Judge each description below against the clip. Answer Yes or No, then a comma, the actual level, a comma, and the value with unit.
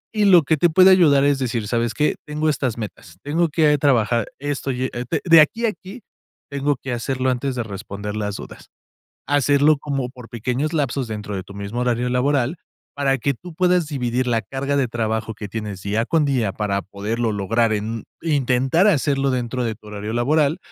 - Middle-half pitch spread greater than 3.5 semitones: Yes, average, 4.5 semitones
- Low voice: Yes, low, 130 Hz